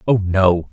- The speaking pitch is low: Yes, low, 100 Hz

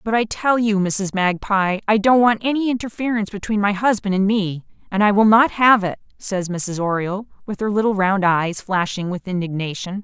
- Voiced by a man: No, female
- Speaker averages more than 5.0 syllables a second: Yes, 5.2 syllables/s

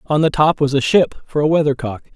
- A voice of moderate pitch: Yes, medium, 145 Hz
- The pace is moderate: No, fast, 250 wpm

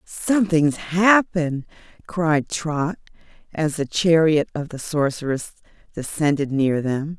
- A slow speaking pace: Yes, slow, 110 wpm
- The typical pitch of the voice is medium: Yes, medium, 155 Hz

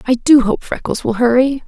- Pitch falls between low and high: No, high, 245 Hz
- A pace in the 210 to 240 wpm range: Yes, fast, 215 wpm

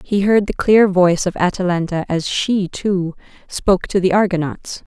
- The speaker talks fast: No, average, 170 wpm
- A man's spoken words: No, female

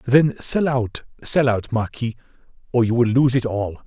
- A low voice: Yes, low, 120 Hz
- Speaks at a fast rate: No, average, 170 wpm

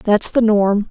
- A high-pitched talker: Yes, high, 210 Hz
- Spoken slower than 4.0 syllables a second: Yes, 3.5 syllables/s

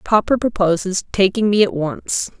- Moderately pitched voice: No, high, 195 Hz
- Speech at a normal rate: Yes, average, 150 wpm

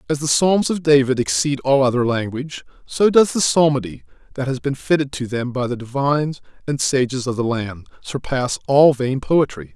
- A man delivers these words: Yes, male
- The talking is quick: No, average, 190 wpm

